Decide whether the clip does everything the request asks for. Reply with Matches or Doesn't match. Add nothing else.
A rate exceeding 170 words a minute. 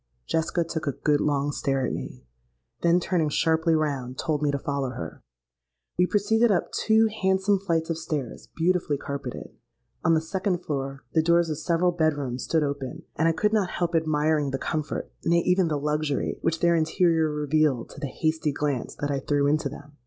Matches